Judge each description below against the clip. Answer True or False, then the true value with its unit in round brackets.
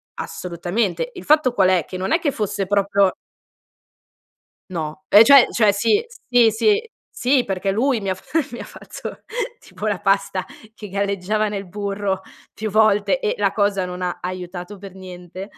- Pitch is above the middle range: True (200 Hz)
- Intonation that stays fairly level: False (3.3 semitones)